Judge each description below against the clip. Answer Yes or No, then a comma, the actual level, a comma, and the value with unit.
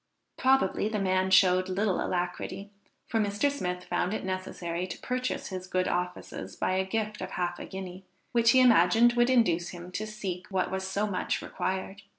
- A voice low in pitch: No, high, 190 Hz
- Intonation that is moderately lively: Yes, average, 3.0 semitones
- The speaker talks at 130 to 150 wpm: No, average, 180 wpm